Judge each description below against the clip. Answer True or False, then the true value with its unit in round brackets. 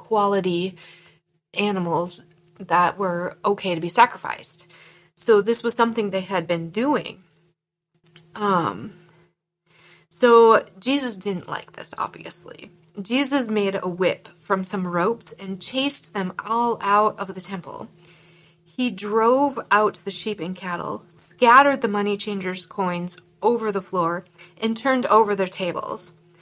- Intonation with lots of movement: False (4.1 semitones)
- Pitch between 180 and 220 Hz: True (190 Hz)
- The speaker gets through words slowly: True (130 wpm)